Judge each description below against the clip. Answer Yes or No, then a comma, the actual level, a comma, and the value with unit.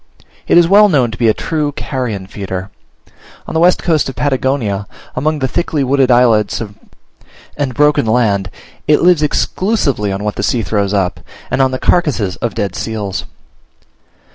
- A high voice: No, low, 125 Hz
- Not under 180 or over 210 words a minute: No, average, 165 wpm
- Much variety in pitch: Yes, wide, 6.1 semitones